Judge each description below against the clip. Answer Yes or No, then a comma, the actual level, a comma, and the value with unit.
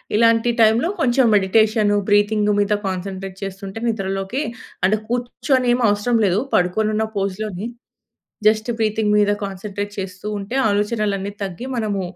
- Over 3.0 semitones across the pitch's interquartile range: No, narrow, 2.4 semitones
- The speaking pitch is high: Yes, high, 205 Hz